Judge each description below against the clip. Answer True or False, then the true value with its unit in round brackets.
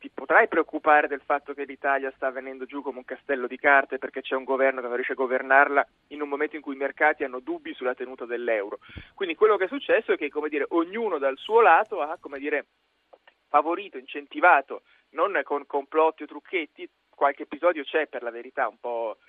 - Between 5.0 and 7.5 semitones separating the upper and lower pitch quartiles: False (3.5 semitones)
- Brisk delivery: True (210 wpm)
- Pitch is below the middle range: False (145 Hz)